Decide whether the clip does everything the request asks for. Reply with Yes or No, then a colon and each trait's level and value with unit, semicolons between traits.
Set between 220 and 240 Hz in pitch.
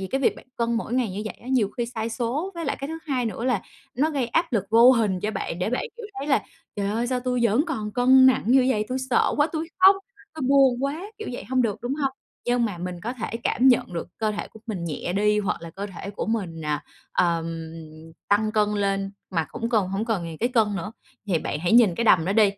Yes: high, 225 Hz